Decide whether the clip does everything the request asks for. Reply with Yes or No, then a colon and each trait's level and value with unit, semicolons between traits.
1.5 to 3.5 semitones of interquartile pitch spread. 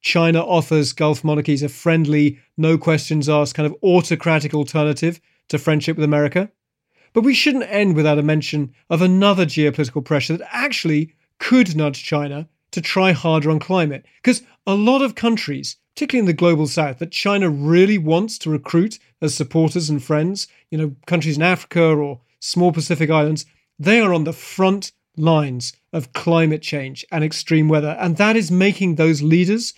Yes: average, 3.2 semitones